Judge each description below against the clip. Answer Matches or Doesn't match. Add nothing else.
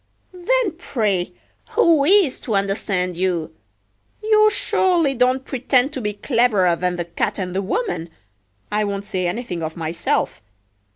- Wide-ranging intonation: Matches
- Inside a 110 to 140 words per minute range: Matches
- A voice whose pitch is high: Matches